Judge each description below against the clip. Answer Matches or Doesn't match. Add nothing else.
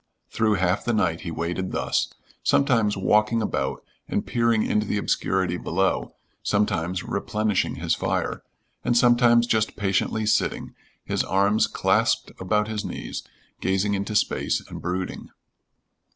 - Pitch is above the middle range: Doesn't match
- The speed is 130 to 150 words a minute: Matches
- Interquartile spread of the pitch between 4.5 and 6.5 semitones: Doesn't match